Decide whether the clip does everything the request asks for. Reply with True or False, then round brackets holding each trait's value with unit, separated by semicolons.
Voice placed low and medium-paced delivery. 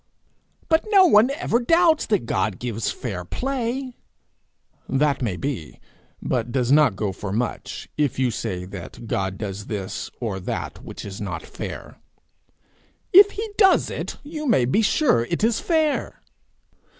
True (130 Hz; 150 wpm)